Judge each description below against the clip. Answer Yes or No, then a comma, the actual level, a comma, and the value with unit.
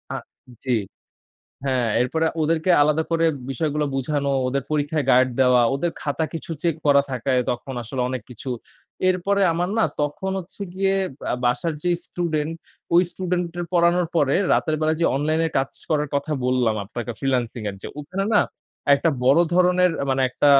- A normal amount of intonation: Yes, average, 4.6 semitones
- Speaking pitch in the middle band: Yes, medium, 150 Hz